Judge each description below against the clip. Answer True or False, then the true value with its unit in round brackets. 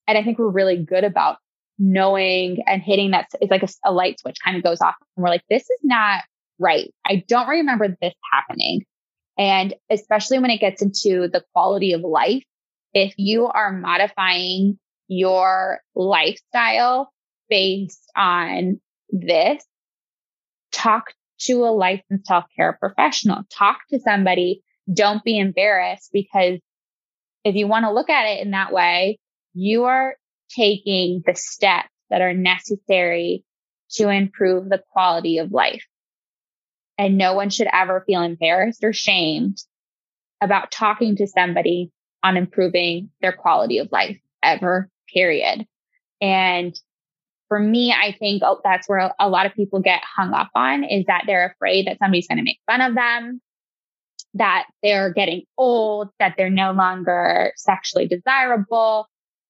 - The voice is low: False (195 Hz)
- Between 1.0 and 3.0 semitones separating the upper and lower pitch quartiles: True (2.6 semitones)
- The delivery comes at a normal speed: True (150 wpm)